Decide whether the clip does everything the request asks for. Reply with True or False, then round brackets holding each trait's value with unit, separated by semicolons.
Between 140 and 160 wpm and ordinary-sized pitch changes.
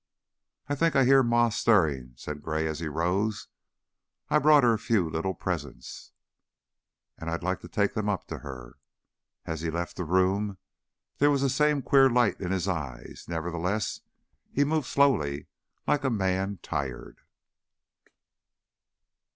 False (150 wpm; 7.0 semitones)